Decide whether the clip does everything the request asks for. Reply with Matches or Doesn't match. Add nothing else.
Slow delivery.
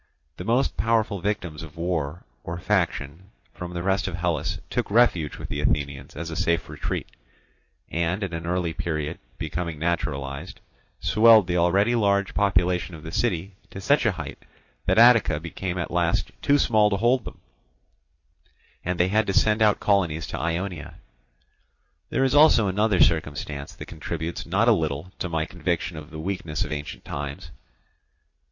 Doesn't match